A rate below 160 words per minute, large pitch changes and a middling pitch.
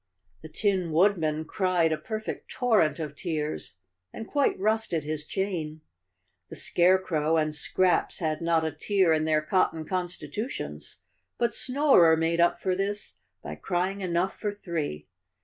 No: average, 150 wpm; average, 3.8 semitones; medium, 175 Hz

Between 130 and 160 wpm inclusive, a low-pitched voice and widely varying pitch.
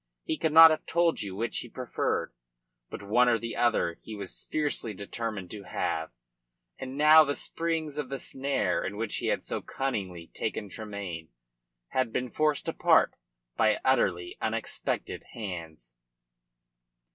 Yes: average, 150 wpm; low, 115 Hz; wide, 6.3 semitones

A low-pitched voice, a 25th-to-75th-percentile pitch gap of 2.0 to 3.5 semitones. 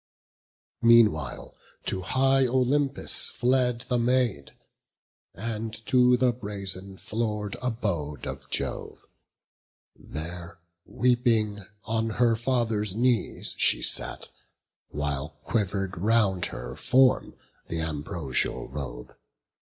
No: low, 110 Hz; wide, 5.6 semitones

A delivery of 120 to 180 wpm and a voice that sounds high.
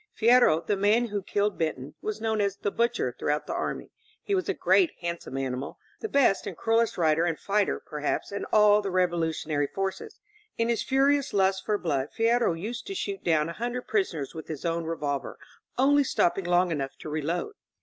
No: average, 195 wpm; high, 195 Hz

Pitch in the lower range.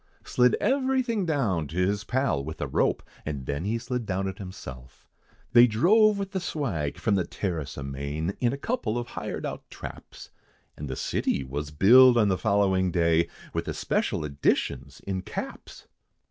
Yes: very low, 95 Hz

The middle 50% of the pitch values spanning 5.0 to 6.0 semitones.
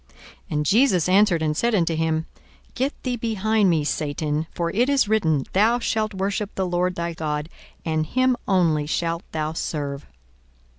Yes: wide, 5.4 semitones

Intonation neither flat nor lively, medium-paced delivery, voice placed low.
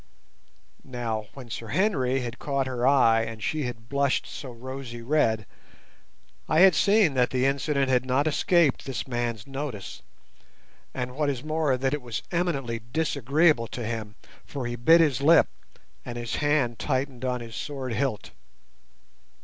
Yes: average, 3.5 semitones; average, 155 wpm; low, 130 Hz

